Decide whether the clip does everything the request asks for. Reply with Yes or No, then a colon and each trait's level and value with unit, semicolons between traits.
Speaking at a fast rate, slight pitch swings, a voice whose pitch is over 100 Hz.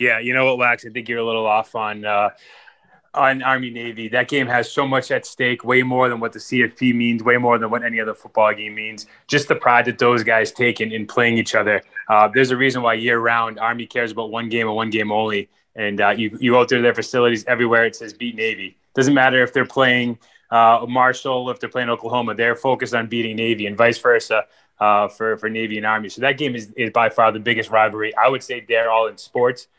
Yes: fast, 245 wpm; narrow, 2.0 semitones; low, 115 Hz